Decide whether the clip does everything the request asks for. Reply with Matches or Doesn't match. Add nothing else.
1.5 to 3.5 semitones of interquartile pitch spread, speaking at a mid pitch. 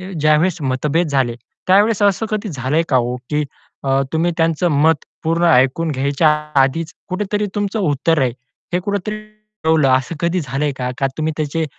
Doesn't match